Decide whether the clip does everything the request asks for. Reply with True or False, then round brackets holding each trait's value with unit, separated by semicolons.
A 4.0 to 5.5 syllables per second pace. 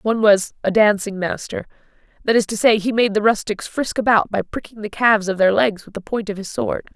False (5.7 syllables/s)